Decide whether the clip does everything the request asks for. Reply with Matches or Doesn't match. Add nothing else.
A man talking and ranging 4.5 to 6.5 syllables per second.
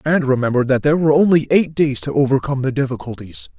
Doesn't match